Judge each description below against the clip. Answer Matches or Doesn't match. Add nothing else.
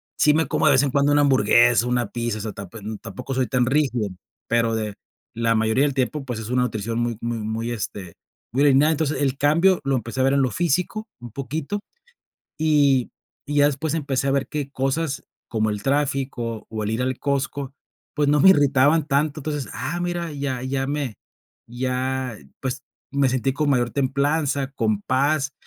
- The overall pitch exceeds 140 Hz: Doesn't match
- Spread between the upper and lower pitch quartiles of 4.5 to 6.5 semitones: Doesn't match